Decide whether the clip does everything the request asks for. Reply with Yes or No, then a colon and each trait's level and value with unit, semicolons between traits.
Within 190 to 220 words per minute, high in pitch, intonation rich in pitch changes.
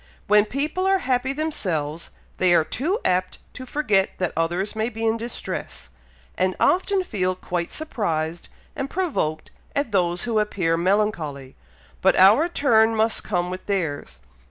No: average, 150 wpm; high, 205 Hz; wide, 6.7 semitones